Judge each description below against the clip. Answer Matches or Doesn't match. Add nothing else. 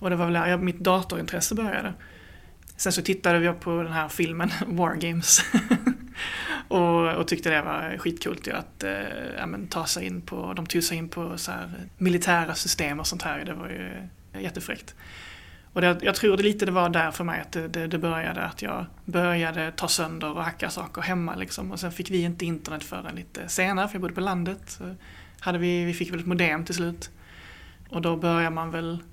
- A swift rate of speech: Matches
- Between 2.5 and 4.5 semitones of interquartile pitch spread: Matches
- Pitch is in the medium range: Matches